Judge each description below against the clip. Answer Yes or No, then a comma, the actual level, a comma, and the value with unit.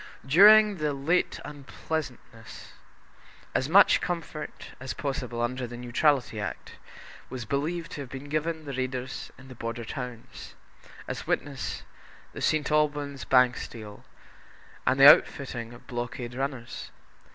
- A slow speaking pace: Yes, slow, 130 wpm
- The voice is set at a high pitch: No, low, 135 Hz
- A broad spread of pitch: No, average, 3.6 semitones